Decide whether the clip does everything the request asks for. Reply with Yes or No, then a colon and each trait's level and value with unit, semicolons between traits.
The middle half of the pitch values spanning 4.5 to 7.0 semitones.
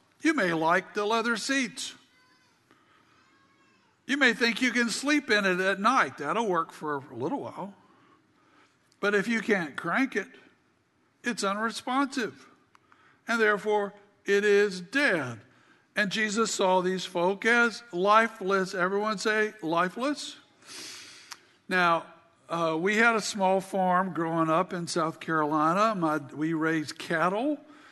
Yes: average, 4.8 semitones